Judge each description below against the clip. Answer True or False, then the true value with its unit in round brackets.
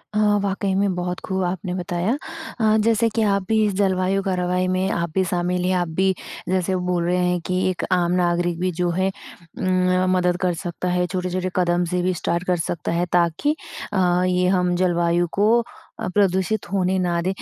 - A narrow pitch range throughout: True (1.3 semitones)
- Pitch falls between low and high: True (180 Hz)